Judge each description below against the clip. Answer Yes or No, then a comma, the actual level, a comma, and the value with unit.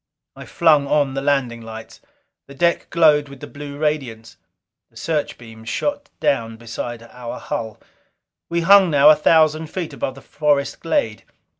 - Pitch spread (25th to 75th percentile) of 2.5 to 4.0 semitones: No, average, 4.9 semitones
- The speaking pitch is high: No, medium, 140 Hz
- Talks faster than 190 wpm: No, average, 155 wpm